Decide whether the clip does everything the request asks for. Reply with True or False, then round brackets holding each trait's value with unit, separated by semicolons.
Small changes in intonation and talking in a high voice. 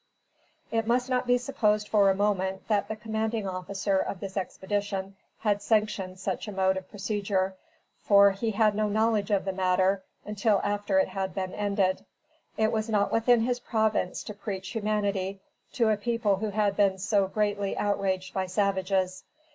True (2.0 semitones; 205 Hz)